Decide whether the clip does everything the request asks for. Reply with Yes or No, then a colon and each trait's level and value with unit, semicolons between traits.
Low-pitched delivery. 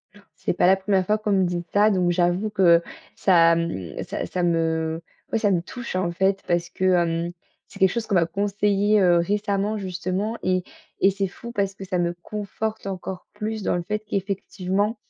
No: high, 190 Hz